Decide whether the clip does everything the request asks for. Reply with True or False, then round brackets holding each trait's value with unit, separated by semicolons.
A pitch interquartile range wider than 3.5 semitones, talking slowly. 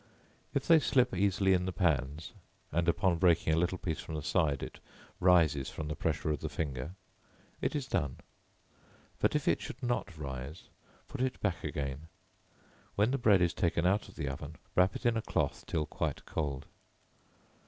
False (4.4 semitones; 185 wpm)